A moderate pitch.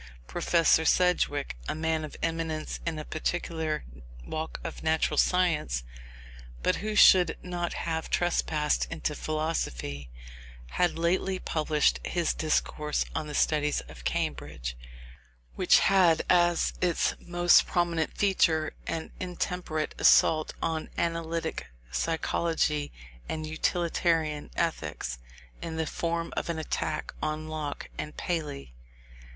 Yes: medium, 160 Hz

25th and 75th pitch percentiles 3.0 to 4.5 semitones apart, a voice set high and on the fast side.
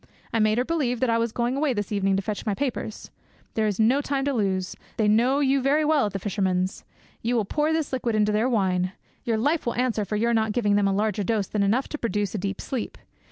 Yes: average, 3.9 semitones; high, 220 Hz; fast, 250 wpm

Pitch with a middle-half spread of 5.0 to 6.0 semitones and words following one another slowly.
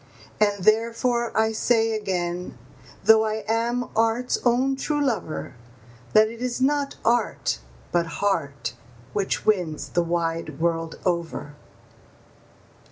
Yes: wide, 5.5 semitones; slow, 115 wpm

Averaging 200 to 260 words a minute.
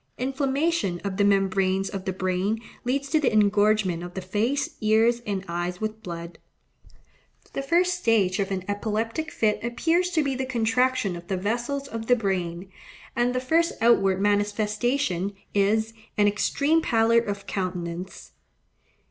No: average, 150 wpm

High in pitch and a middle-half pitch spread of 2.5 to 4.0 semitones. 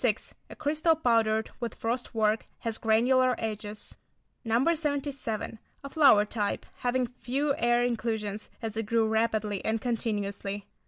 Yes: high, 230 Hz; average, 2.8 semitones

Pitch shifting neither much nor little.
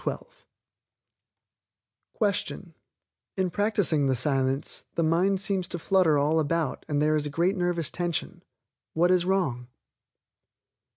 Yes: average, 4.0 semitones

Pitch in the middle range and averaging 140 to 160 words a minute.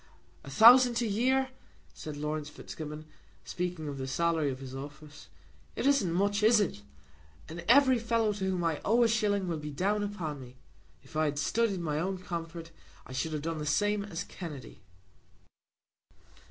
No: medium, 170 Hz; average, 175 wpm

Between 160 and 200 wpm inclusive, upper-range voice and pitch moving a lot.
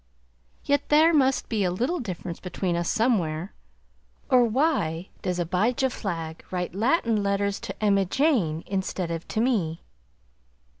No: average, 140 wpm; high, 200 Hz; wide, 6.2 semitones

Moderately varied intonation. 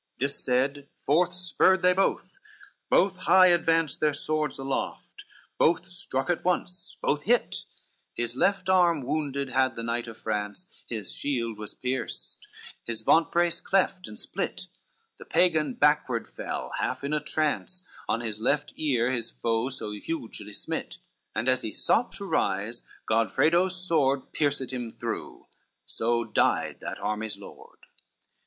No: wide, 6.7 semitones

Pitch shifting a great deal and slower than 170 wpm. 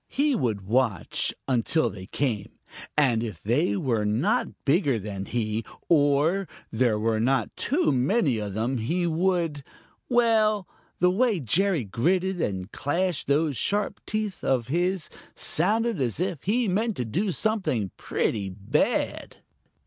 Yes: wide, 8.9 semitones; average, 145 wpm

